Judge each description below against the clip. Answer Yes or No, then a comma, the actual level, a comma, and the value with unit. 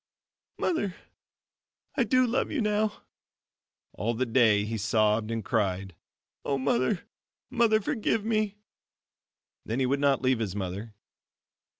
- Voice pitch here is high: No, low, 130 Hz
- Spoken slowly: Yes, slow, 125 wpm